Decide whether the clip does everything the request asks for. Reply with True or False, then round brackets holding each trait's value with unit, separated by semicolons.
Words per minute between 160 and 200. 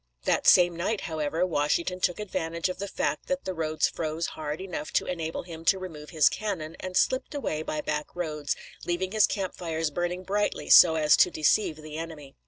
True (195 wpm)